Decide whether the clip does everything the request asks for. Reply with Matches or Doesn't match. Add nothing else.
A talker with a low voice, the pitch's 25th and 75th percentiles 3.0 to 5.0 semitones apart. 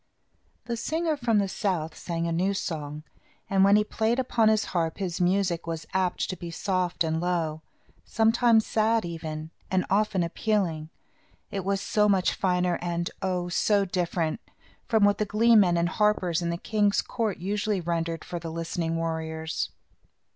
Doesn't match